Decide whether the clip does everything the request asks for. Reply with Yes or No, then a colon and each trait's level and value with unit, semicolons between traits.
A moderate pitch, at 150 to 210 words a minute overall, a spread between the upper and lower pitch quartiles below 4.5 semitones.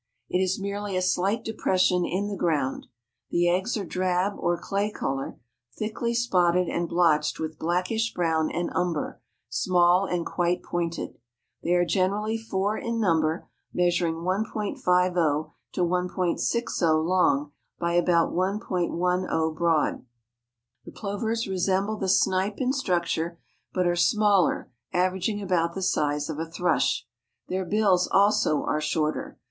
No: medium, 180 Hz; slow, 135 wpm; average, 2.8 semitones